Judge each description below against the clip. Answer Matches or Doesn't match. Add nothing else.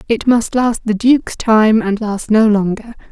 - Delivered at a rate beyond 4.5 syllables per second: Doesn't match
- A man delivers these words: Doesn't match